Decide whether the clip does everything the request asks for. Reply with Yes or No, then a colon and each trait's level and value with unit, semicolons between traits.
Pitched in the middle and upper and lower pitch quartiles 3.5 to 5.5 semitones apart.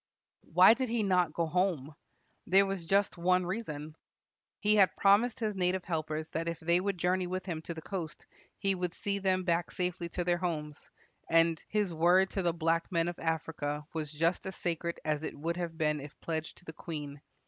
No: medium, 175 Hz; average, 2.7 semitones